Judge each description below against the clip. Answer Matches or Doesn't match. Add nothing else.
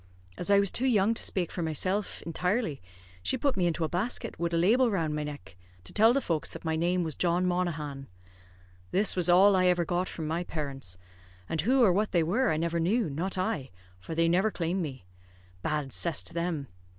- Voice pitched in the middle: Matches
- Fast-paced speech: Matches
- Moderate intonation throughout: Matches